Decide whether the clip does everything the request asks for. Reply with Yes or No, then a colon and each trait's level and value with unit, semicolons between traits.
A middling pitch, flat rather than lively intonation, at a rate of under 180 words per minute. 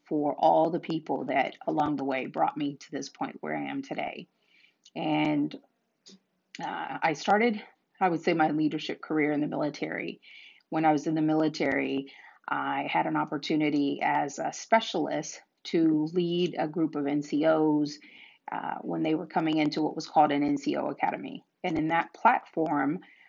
Yes: medium, 155 Hz; narrow, 2.0 semitones; average, 165 wpm